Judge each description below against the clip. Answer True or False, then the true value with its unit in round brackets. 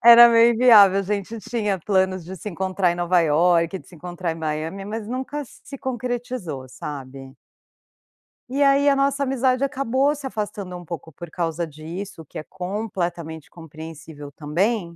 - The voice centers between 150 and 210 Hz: True (190 Hz)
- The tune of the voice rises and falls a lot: True (6.3 semitones)